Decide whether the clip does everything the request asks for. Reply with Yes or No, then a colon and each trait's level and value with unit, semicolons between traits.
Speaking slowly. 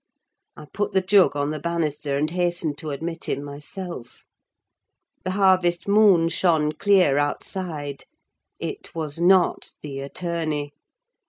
Yes: slow, 130 wpm